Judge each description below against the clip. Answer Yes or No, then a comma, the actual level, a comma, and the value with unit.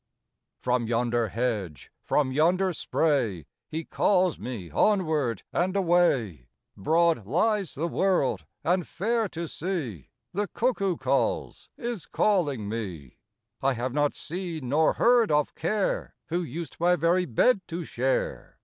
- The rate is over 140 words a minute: No, slow, 135 wpm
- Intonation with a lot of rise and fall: Yes, wide, 7.2 semitones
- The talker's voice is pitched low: No, medium, 165 Hz